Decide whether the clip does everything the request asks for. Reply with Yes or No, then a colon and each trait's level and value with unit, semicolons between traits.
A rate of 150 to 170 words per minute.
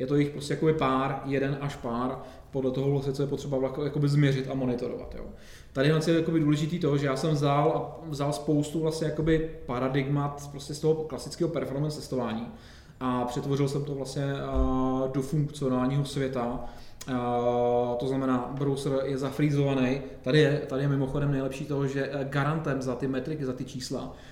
Yes: average, 165 wpm